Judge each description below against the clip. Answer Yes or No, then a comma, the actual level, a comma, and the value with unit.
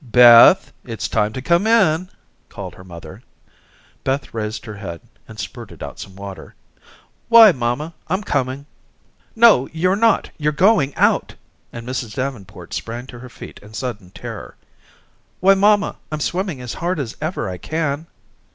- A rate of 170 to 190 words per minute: No, average, 155 wpm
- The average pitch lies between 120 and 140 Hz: Yes, low, 135 Hz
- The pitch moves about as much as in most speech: No, wide, 7.3 semitones